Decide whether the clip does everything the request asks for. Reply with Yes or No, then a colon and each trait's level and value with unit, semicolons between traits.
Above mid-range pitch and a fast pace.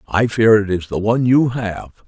No: low, 110 Hz; fast, 230 wpm